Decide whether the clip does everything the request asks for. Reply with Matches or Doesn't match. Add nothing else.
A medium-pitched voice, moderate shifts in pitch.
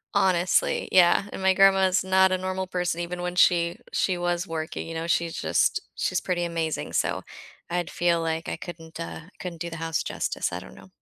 Doesn't match